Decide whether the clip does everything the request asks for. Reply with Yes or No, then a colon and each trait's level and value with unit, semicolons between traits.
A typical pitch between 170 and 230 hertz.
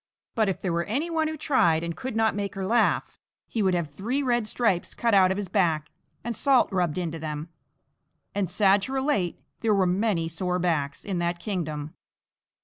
Yes: high, 190 Hz